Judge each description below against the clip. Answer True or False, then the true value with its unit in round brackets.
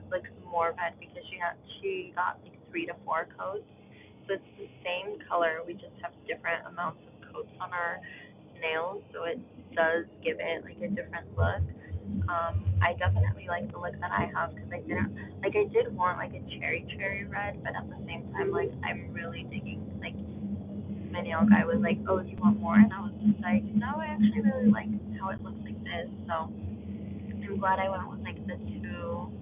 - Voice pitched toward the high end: False (140 Hz)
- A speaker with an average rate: False (210 wpm)